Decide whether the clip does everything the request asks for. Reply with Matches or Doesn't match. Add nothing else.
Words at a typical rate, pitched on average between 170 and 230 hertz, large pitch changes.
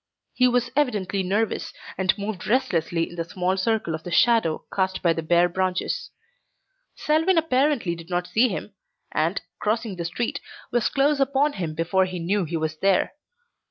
Matches